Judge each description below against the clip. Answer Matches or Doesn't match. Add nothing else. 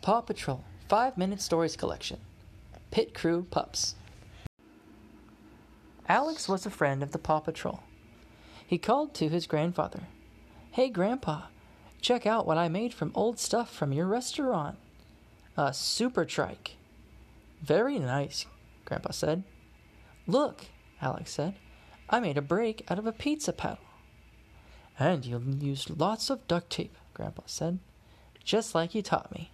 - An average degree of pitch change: Doesn't match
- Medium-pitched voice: Matches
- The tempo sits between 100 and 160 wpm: Matches